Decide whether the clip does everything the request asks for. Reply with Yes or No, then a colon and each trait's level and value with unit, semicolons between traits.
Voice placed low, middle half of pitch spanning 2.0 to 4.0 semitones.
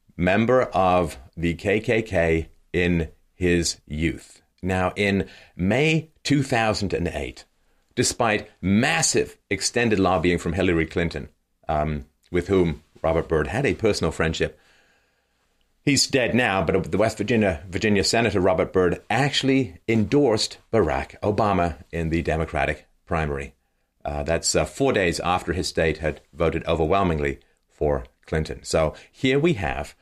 No: very low, 90 Hz; average, 4.6 semitones